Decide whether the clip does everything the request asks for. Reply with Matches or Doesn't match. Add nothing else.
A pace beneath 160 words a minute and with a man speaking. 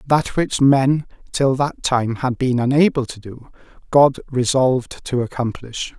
Matches